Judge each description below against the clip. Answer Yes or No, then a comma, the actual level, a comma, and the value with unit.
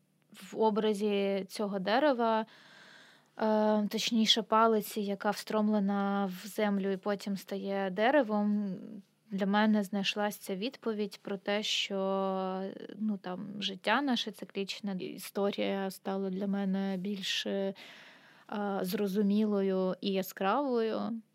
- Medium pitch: No, high, 205 Hz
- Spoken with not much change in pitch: Yes, narrow, 1.7 semitones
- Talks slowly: Yes, slow, 95 wpm